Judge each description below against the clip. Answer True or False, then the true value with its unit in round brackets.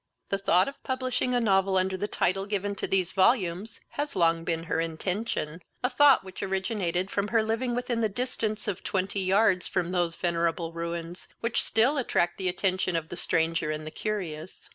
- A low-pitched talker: False (190 Hz)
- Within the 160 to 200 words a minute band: True (185 wpm)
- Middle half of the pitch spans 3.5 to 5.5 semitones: True (4.3 semitones)